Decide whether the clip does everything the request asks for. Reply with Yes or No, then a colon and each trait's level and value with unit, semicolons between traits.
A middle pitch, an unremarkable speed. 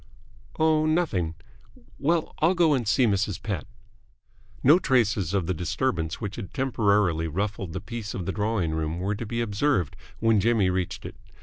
No: low, 105 Hz; average, 170 wpm